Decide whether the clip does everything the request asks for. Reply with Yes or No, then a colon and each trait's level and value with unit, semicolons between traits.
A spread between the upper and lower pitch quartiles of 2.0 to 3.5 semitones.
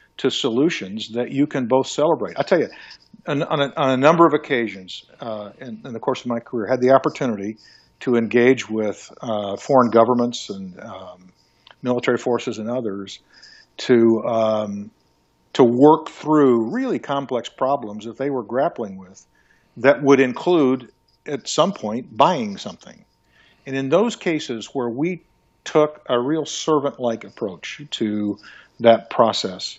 No: average, 4.0 semitones